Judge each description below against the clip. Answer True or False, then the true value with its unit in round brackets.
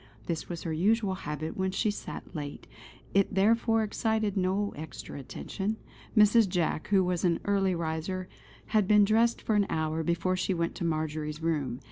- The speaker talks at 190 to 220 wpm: False (170 wpm)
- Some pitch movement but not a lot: True (4.4 semitones)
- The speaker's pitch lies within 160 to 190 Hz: True (185 Hz)